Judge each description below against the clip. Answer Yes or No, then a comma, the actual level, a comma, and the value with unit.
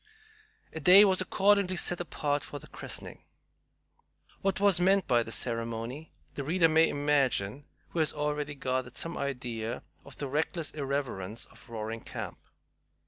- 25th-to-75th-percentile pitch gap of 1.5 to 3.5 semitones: No, wide, 5.4 semitones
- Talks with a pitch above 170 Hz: No, medium, 145 Hz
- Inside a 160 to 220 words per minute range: No, average, 145 wpm